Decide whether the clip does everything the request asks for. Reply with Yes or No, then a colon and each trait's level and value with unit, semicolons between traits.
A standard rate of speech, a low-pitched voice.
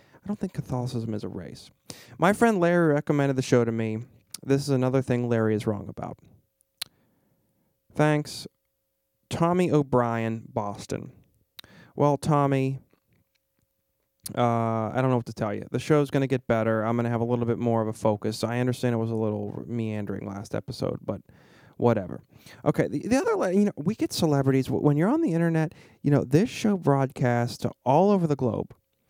Yes: average, 180 wpm; low, 125 Hz